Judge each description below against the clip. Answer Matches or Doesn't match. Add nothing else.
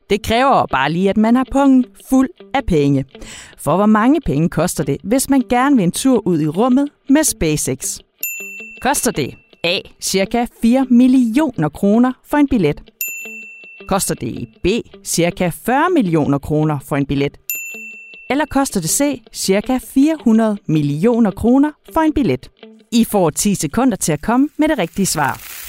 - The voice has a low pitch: Doesn't match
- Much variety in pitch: Matches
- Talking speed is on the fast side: Doesn't match